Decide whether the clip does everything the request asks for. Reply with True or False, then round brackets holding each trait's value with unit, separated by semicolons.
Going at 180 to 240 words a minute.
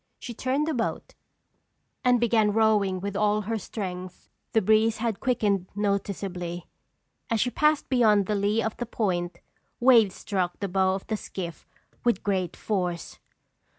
False (150 wpm)